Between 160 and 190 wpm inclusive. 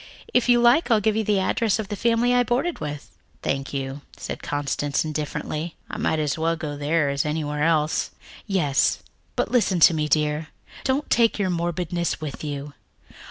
Yes: average, 180 wpm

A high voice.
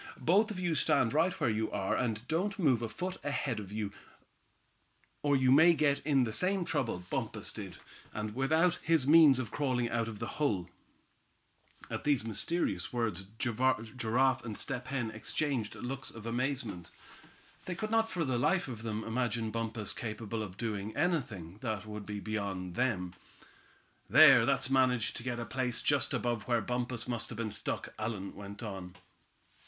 No: low, 120 Hz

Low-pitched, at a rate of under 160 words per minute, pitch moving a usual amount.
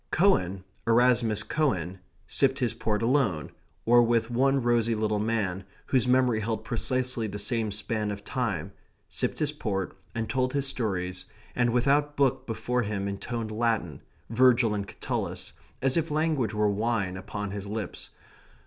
Yes: low, 115 Hz; average, 150 wpm; average, 3.6 semitones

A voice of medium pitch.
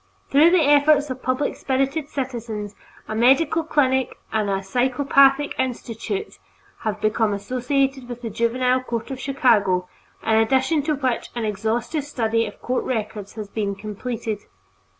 No: very high, 250 Hz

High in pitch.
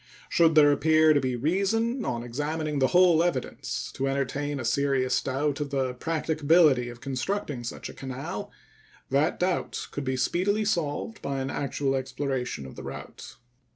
No: medium, 145 Hz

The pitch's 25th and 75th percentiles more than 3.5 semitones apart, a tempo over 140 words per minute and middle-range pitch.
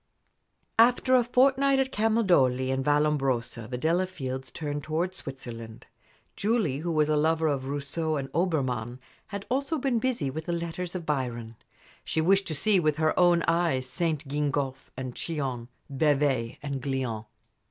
Yes: average, 5.2 semitones; average, 150 wpm; medium, 150 Hz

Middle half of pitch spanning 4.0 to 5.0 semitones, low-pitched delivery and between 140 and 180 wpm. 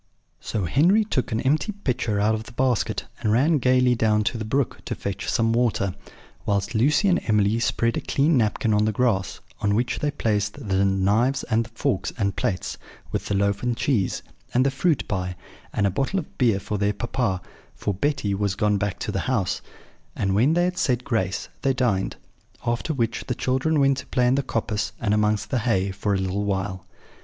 No: average, 4.3 semitones; low, 115 Hz; fast, 205 wpm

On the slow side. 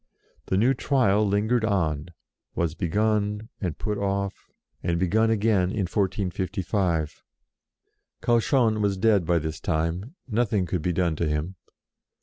Yes: slow, 130 wpm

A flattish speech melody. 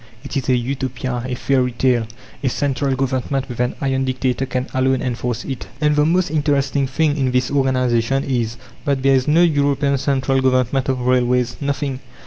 Yes: narrow, 1.7 semitones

